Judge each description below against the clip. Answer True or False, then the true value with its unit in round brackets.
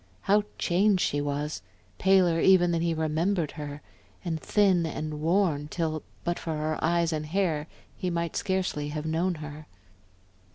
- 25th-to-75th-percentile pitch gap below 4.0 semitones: True (2.9 semitones)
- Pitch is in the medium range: True (165 Hz)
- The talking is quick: False (155 wpm)